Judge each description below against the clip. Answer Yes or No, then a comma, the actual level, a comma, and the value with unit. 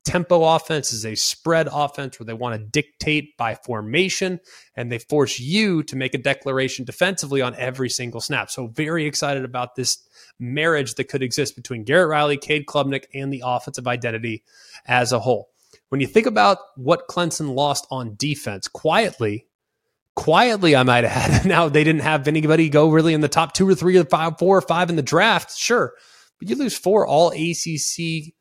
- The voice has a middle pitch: Yes, medium, 145 Hz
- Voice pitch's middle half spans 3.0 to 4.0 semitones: No, average, 4.4 semitones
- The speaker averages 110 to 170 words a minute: No, average, 190 wpm